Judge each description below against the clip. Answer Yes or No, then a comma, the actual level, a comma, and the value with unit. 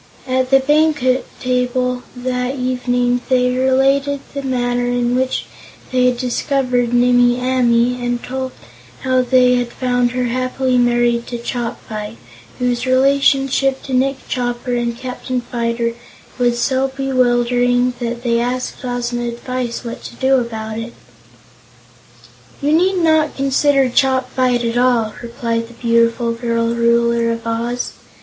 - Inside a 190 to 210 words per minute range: No, slow, 135 wpm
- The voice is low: No, very high, 250 Hz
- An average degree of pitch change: No, narrow, 1.4 semitones